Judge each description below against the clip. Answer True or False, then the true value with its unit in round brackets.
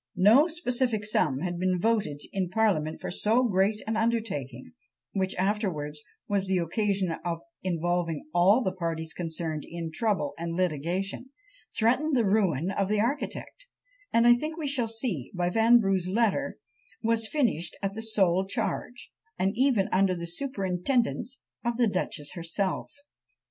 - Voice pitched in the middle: False (195 Hz)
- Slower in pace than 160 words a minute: True (150 wpm)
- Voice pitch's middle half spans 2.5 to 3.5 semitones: False (4.9 semitones)